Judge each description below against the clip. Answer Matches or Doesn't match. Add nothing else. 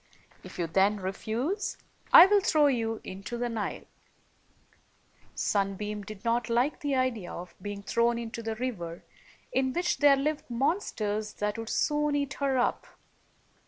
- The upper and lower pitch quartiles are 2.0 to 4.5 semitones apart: Doesn't match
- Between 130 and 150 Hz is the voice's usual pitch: Doesn't match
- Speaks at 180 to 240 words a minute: Doesn't match